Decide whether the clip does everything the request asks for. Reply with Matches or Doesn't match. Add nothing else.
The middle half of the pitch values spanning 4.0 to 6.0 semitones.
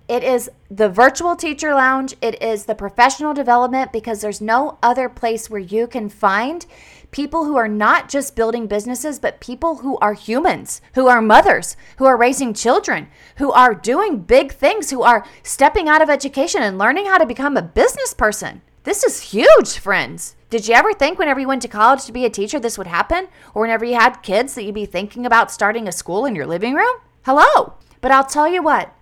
Matches